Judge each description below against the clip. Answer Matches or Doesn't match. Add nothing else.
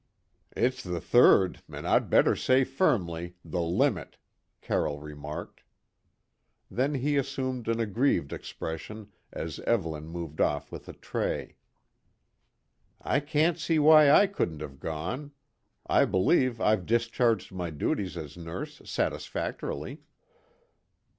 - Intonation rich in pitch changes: Matches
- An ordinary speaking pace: Doesn't match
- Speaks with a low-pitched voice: Matches